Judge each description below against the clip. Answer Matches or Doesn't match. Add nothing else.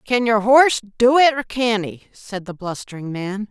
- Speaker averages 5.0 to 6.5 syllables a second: Doesn't match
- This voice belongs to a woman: Matches